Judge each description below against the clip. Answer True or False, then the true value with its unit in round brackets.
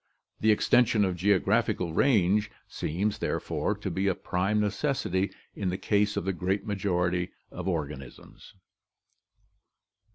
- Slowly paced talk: True (130 wpm)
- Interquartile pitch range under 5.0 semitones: True (2.7 semitones)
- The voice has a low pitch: True (95 Hz)